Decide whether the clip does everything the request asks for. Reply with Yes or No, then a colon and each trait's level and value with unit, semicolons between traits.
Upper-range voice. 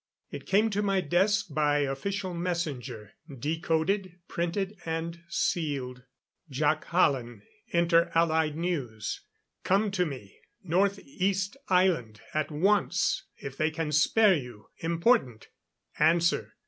No: medium, 165 Hz